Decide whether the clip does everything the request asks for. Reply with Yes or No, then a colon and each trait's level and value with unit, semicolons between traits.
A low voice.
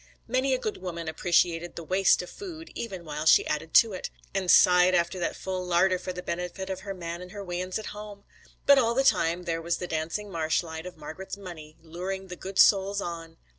No: medium, 180 Hz